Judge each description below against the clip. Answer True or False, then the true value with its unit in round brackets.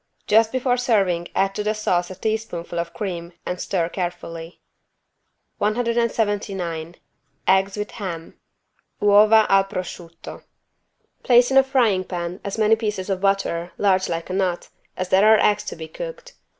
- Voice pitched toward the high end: True (195 Hz)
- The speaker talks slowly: False (150 wpm)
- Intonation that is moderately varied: True (3.7 semitones)